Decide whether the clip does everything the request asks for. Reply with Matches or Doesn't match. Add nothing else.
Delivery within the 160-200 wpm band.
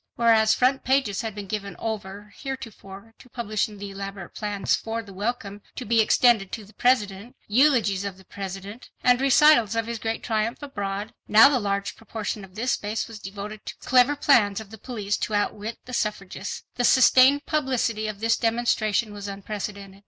Matches